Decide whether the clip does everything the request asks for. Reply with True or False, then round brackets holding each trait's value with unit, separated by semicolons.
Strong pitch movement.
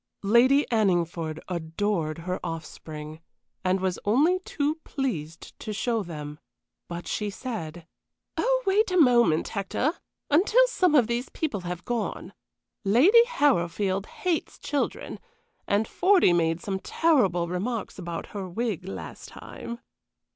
True (8.3 semitones)